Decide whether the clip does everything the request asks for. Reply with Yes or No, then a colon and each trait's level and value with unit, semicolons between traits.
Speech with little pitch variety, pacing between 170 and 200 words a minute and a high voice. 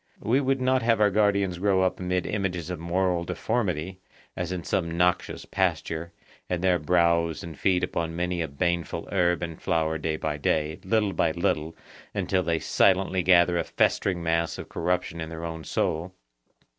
No: narrow, 2.1 semitones; average, 175 wpm; very low, 85 Hz